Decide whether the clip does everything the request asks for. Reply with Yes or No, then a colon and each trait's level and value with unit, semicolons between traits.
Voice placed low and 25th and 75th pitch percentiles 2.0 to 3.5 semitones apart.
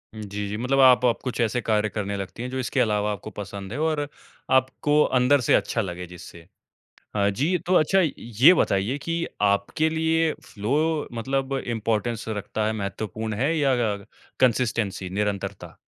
No: low, 115 Hz; average, 5.0 semitones